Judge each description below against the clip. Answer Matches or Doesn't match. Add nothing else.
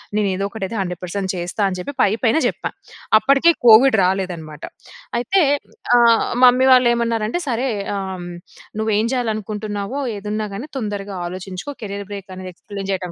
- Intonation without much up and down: Doesn't match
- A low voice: Doesn't match